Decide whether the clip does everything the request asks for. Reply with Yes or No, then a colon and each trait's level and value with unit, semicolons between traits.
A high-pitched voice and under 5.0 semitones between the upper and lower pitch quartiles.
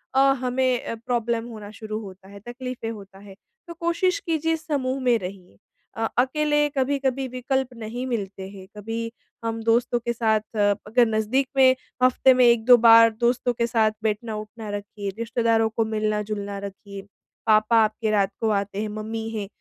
Yes: high, 225 Hz; average, 3.0 semitones